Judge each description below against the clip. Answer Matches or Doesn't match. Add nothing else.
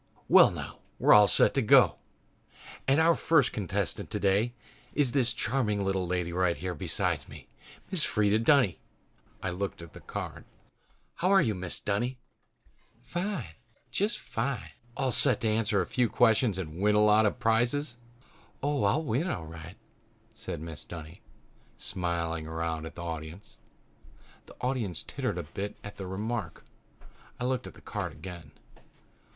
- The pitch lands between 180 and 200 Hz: Doesn't match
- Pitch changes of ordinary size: Doesn't match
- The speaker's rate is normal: Matches